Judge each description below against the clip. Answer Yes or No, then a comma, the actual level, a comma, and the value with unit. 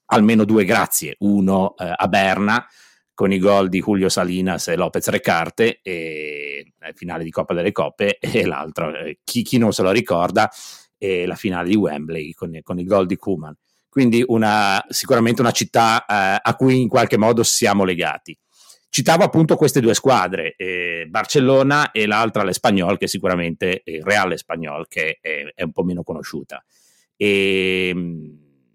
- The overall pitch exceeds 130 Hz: No, low, 100 Hz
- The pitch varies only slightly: No, average, 4.6 semitones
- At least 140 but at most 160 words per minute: No, fast, 170 wpm